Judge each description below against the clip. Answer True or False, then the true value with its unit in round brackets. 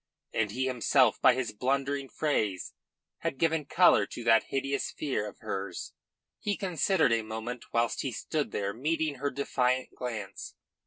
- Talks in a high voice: False (130 Hz)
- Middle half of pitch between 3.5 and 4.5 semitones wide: True (4.1 semitones)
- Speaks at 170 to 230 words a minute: False (155 wpm)